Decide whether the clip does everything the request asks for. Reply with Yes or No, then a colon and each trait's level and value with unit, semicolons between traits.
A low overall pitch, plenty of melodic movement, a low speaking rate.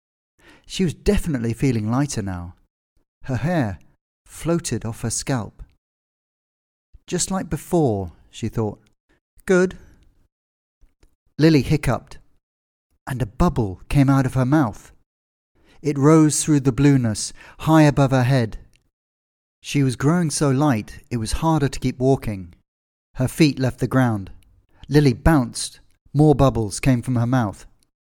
Yes: low, 120 Hz; wide, 8.0 semitones; slow, 130 wpm